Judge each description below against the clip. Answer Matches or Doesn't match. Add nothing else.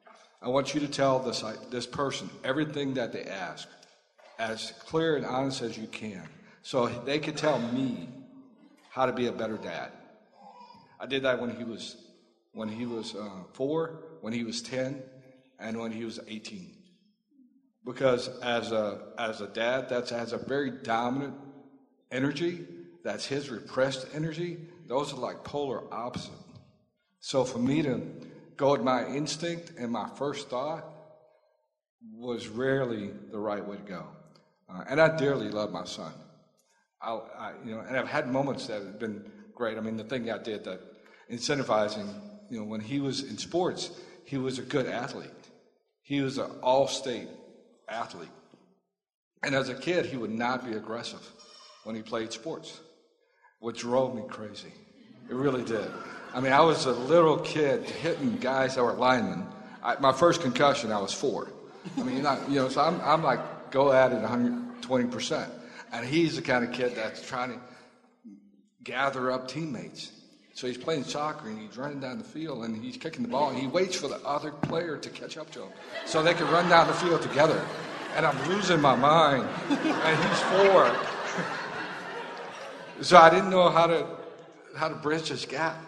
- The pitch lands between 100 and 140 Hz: Matches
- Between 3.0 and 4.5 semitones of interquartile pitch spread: Doesn't match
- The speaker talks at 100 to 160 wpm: Doesn't match